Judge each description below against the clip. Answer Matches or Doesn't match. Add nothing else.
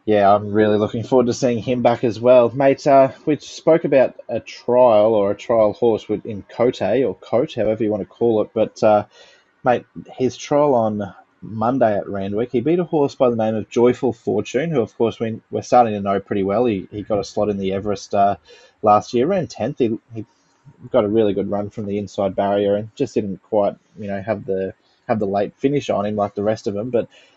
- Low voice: Matches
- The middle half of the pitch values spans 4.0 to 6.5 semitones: Doesn't match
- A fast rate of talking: Matches